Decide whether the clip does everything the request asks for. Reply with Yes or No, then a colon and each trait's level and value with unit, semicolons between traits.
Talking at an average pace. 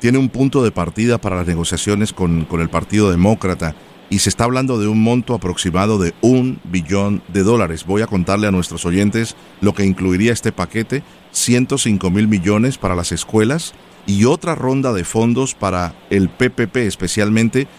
Yes: average, 175 wpm